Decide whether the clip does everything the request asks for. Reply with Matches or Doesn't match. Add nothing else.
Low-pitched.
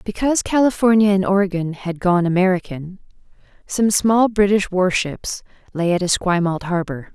Doesn't match